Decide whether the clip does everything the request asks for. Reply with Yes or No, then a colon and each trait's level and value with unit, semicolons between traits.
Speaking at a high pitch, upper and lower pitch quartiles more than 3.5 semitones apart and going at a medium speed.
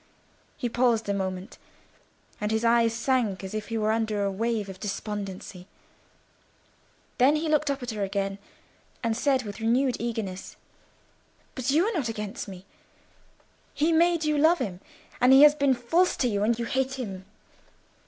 Yes: high, 230 Hz; average, 4.7 semitones; average, 165 wpm